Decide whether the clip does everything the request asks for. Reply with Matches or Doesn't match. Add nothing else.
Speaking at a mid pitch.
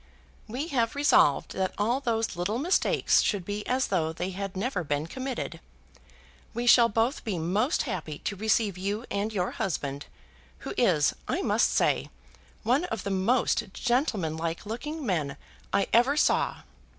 Doesn't match